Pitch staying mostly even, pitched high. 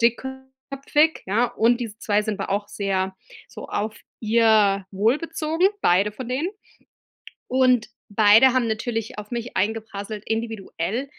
No: average, 3.7 semitones; high, 225 Hz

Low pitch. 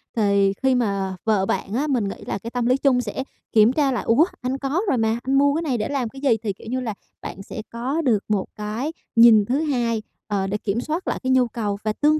No: high, 235 Hz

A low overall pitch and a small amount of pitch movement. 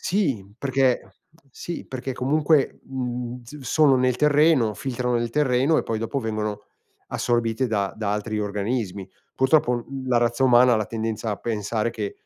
No: low, 125 Hz; average, 3.2 semitones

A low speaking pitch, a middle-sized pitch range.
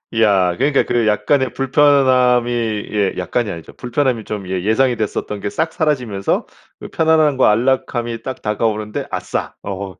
Yes: low, 115 Hz; average, 4.1 semitones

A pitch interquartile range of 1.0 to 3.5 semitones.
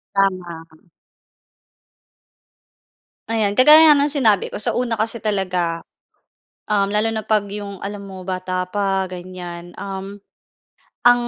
Yes: average, 3.0 semitones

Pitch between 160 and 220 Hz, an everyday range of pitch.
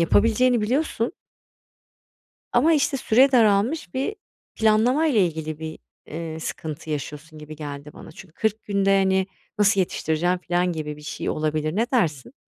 No: medium, 185 Hz; wide, 6.6 semitones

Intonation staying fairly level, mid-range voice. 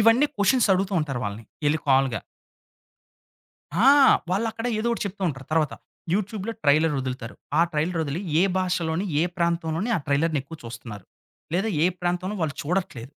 No: wide, 5.6 semitones; medium, 165 Hz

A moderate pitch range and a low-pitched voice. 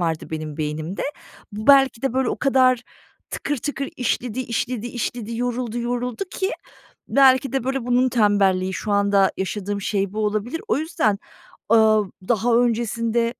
No: average, 3.7 semitones; high, 230 Hz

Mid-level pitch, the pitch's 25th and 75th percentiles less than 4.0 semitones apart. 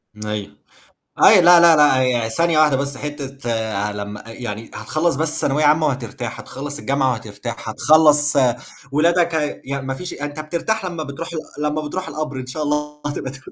Yes: medium, 145 Hz; average, 3.3 semitones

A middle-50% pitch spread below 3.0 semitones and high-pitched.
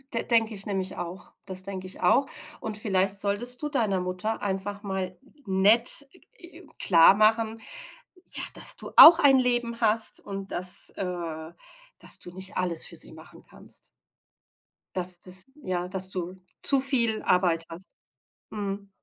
No: average, 3.5 semitones; high, 195 Hz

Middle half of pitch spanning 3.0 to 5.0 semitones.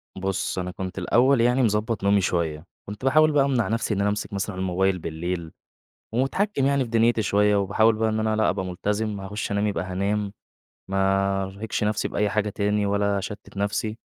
No: narrow, 2.4 semitones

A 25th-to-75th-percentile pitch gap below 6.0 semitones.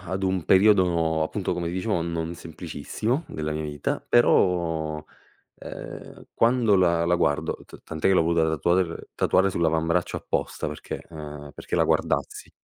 Yes: average, 2.8 semitones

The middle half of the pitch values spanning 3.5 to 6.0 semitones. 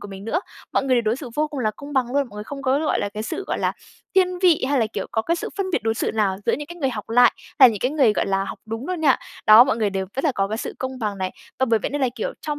Yes: average, 5.1 semitones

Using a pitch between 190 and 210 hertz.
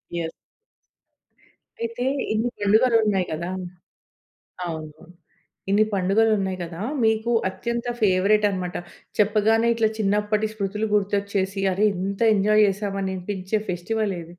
Yes: high, 205 Hz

